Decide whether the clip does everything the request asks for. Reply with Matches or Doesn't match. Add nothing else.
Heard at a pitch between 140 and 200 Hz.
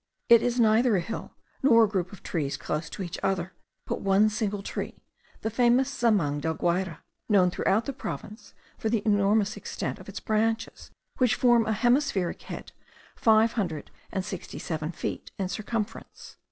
Doesn't match